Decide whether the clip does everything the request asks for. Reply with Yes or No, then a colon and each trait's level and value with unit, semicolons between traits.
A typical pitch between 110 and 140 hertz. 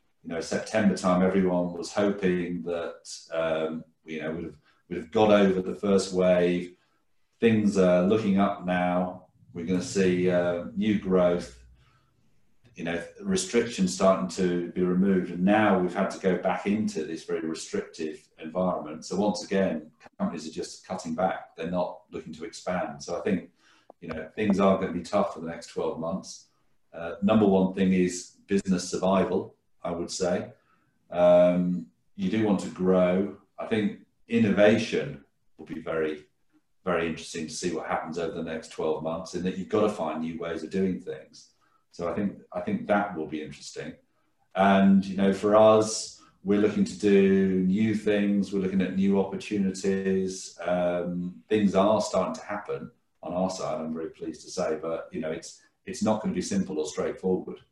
No: very low, 95 Hz